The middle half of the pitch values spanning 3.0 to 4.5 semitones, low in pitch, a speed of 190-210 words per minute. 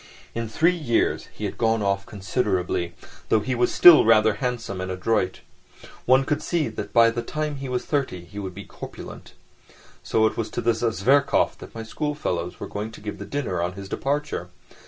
No: average, 5.1 semitones; low, 115 Hz; average, 195 wpm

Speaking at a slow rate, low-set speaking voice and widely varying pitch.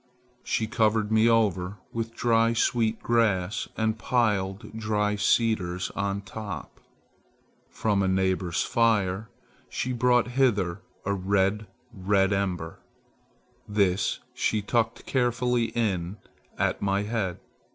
No: slow, 110 wpm; low, 105 Hz; average, 3.0 semitones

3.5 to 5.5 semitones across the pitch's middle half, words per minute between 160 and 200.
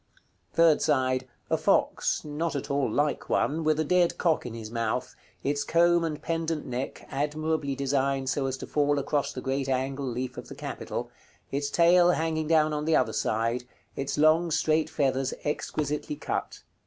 No: average, 3.0 semitones; average, 175 wpm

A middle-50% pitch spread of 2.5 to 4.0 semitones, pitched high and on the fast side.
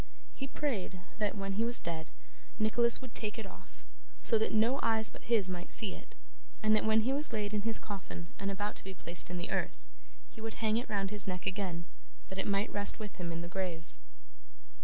Yes: average, 2.9 semitones; high, 205 Hz; fast, 220 wpm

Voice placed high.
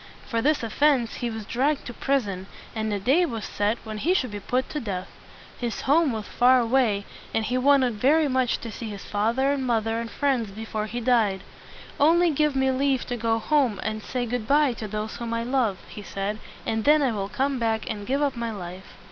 Yes: high, 235 Hz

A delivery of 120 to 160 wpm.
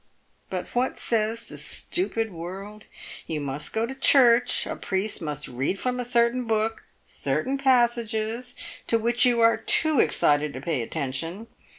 Yes: average, 155 wpm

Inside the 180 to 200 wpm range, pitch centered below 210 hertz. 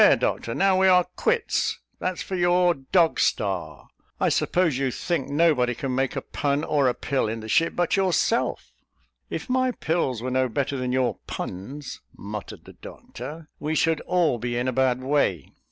Yes: average, 185 wpm; medium, 140 Hz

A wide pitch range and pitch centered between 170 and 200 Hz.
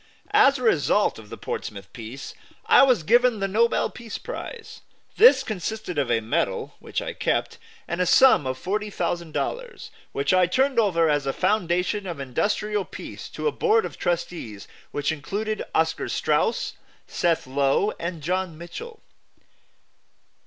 Yes: wide, 6.9 semitones; medium, 185 Hz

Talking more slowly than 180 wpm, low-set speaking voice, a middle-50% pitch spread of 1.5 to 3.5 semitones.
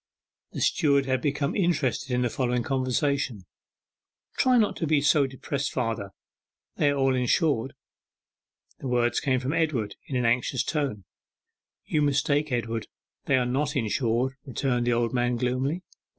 Yes: average, 150 wpm; low, 130 Hz; average, 2.8 semitones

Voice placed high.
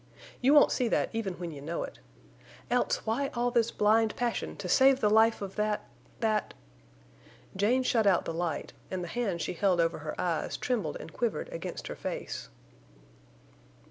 Yes: high, 210 Hz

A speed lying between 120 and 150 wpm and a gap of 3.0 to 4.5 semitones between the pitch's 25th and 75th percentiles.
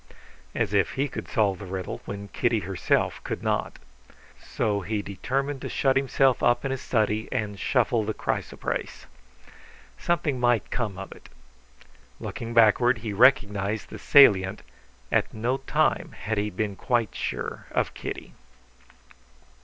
Yes: average, 145 wpm; average, 3.7 semitones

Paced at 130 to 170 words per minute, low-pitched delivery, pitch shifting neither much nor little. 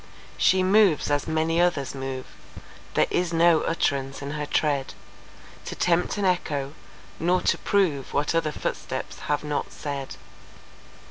No: average, 140 wpm; medium, 155 Hz; average, 3.7 semitones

